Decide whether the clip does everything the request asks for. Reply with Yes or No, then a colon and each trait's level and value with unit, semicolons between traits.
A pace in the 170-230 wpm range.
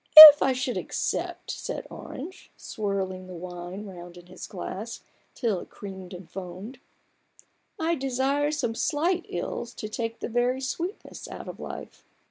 No: average, 160 wpm